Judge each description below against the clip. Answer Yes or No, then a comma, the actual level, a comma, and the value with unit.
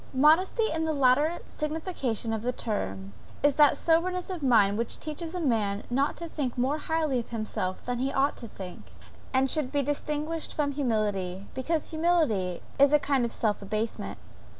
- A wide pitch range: Yes, wide, 5.9 semitones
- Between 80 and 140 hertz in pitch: No, very high, 270 Hz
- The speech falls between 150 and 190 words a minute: Yes, average, 175 wpm